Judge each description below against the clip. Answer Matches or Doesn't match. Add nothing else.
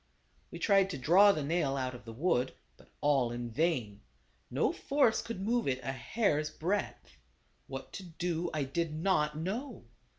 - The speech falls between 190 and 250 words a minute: Doesn't match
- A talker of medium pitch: Matches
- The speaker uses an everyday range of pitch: Doesn't match